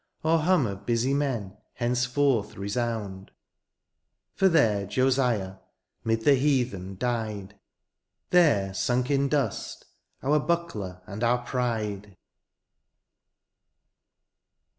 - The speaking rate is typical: No, slow, 95 wpm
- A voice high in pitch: No, low, 120 Hz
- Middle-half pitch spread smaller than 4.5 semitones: No, average, 5.2 semitones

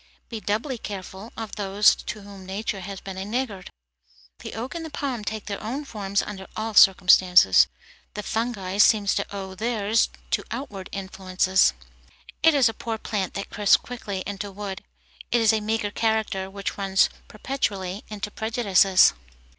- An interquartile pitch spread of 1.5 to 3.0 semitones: Yes, narrow, 2.6 semitones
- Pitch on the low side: No, high, 205 Hz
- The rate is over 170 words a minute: No, average, 160 wpm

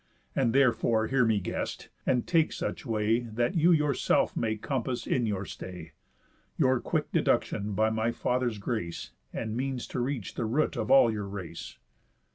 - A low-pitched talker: Yes, low, 115 Hz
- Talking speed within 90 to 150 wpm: No, average, 165 wpm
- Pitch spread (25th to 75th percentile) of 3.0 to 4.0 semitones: Yes, average, 3.3 semitones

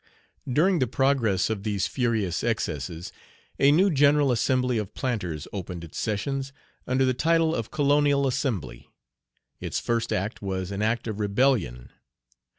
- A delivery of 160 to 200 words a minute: No, average, 145 wpm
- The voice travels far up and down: Yes, wide, 5.9 semitones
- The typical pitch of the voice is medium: No, low, 115 Hz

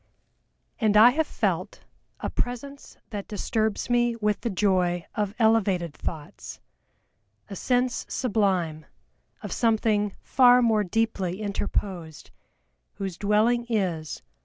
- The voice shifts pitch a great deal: No, average, 3.9 semitones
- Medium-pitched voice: No, high, 210 Hz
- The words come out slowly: Yes, slow, 110 wpm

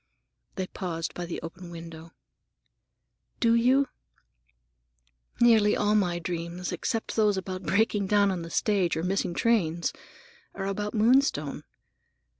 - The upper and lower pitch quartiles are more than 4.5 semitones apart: No, average, 3.7 semitones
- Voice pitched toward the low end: No, high, 190 Hz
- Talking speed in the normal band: No, slow, 125 wpm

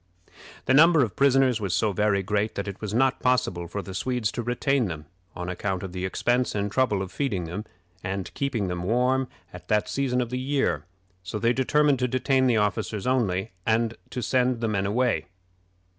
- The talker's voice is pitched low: Yes, low, 110 Hz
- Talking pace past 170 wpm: Yes, average, 200 wpm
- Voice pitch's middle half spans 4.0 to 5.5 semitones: Yes, average, 4.8 semitones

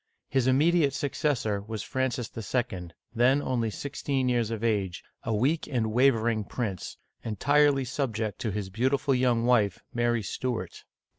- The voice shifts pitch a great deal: No, average, 3.5 semitones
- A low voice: Yes, low, 120 Hz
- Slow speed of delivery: No, average, 145 wpm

